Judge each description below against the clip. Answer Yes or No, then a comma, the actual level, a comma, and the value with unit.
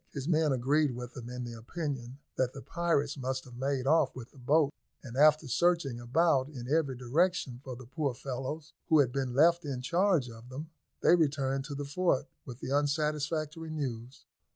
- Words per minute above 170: Yes, average, 190 wpm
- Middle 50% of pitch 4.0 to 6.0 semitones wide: No, average, 3.4 semitones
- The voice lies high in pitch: No, medium, 140 Hz